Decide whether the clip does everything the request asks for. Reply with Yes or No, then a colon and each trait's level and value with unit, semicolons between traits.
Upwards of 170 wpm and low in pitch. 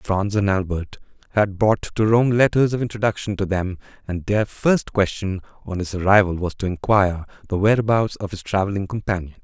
Yes: average, 180 wpm; low, 100 Hz